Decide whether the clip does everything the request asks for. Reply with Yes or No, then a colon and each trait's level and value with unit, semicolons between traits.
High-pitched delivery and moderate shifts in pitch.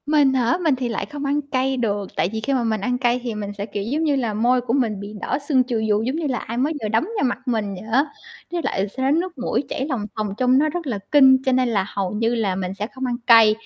Yes: high, 245 Hz; average, 4.0 semitones